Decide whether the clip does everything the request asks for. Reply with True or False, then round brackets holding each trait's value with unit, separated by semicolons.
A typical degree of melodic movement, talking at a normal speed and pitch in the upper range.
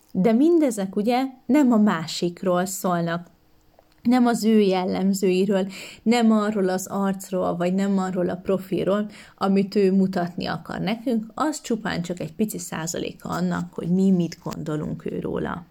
True (3.3 semitones; 145 wpm; 195 Hz)